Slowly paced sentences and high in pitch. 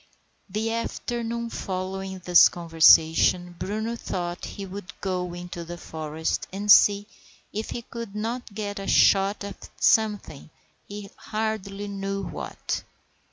Yes: slow, 125 wpm; high, 195 Hz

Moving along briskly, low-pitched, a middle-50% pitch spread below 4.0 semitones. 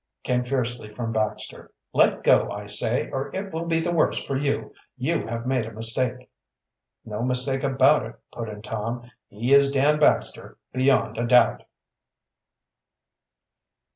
No: average, 150 wpm; low, 125 Hz; average, 3.3 semitones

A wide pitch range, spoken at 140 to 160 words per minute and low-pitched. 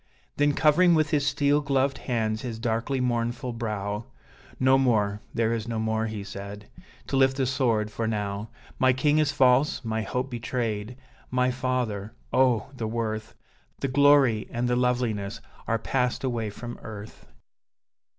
No: average, 3.3 semitones; average, 155 wpm; low, 120 Hz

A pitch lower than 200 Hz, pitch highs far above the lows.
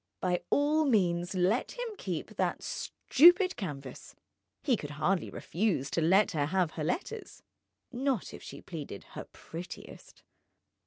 Yes: medium, 185 Hz; wide, 8.6 semitones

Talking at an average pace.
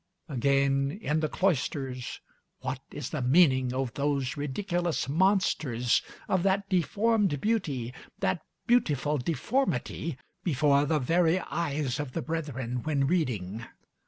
No: slow, 120 wpm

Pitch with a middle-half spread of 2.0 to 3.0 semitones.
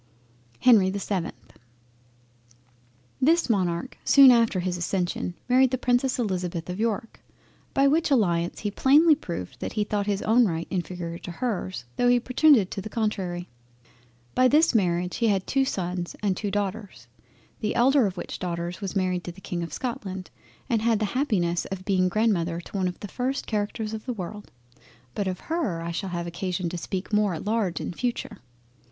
No: average, 4.8 semitones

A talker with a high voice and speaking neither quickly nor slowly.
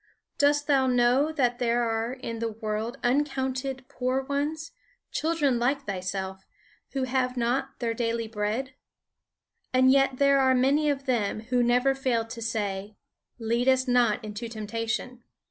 Yes: very high, 250 Hz; average, 145 wpm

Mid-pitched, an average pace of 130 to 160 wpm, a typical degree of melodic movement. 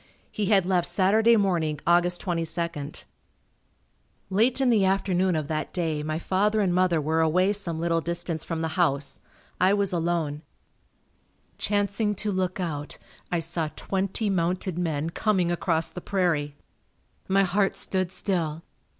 Yes: medium, 175 Hz; average, 145 wpm; average, 3.0 semitones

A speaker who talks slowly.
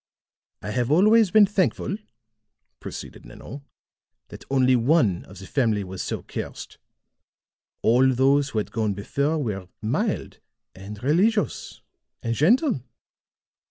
Yes: slow, 125 wpm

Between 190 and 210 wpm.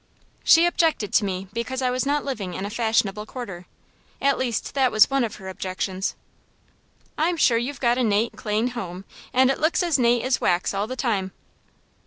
Yes: average, 195 wpm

